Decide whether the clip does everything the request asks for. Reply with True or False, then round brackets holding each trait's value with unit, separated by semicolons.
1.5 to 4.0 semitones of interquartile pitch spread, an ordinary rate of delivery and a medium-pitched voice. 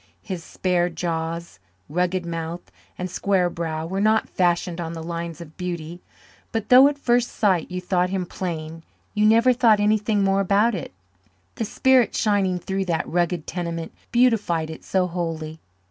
True (3.5 semitones; 160 wpm; 180 Hz)